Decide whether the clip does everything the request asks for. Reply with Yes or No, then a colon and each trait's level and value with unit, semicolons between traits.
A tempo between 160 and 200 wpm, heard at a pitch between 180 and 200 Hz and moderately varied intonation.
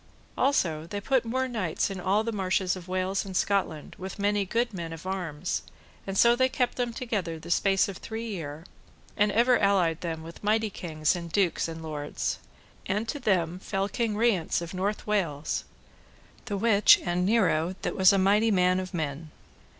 Yes: average, 185 wpm; high, 190 Hz; average, 3.8 semitones